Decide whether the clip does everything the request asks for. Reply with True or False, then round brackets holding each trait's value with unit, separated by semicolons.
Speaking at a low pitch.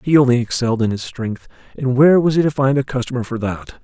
True (125 Hz)